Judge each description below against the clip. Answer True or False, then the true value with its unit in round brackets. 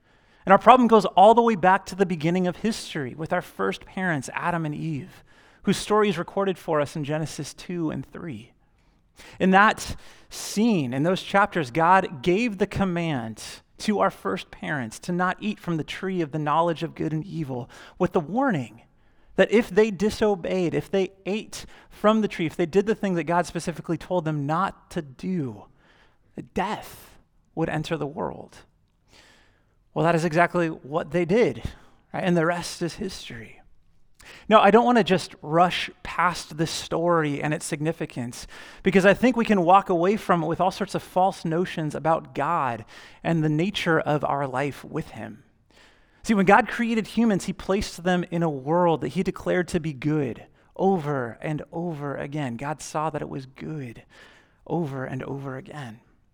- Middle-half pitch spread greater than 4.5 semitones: False (4.0 semitones)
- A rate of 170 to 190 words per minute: True (180 wpm)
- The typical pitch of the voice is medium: True (170 Hz)